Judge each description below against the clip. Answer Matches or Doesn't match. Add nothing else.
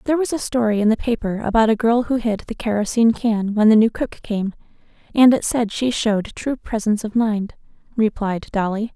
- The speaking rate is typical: Doesn't match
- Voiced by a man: Doesn't match